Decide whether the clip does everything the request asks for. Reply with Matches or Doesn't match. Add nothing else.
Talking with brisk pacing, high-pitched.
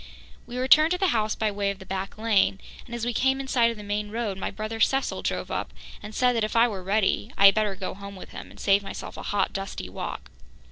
Matches